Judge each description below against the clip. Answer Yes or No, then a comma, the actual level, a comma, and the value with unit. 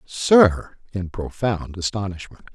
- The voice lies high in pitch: No, low, 100 Hz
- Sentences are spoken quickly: No, slow, 95 wpm